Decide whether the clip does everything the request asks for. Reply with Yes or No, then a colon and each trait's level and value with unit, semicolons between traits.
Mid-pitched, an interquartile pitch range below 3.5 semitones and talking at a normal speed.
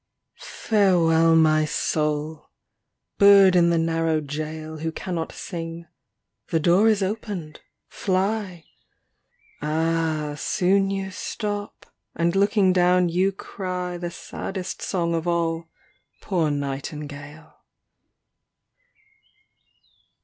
No: medium, 170 Hz; average, 3.0 semitones; slow, 100 wpm